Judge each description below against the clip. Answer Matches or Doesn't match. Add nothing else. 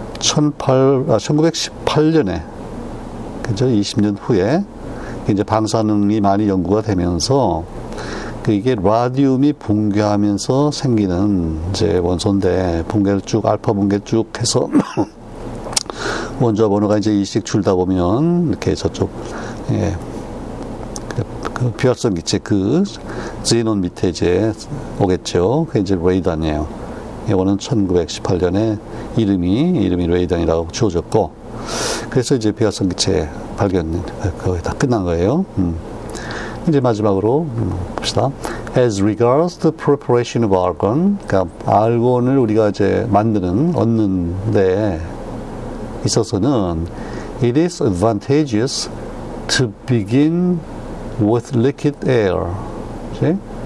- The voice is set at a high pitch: Doesn't match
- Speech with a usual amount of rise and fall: Matches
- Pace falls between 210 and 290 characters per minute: Matches